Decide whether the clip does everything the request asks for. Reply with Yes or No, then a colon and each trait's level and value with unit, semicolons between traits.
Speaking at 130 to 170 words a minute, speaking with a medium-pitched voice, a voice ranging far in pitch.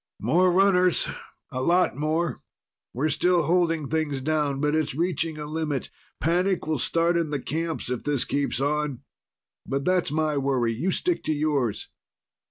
No: average, 160 wpm; medium, 155 Hz; average, 3.3 semitones